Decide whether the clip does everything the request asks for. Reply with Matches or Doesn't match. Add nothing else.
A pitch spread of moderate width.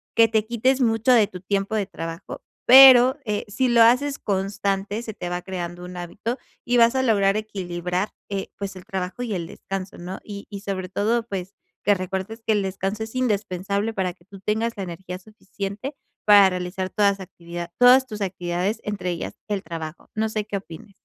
Matches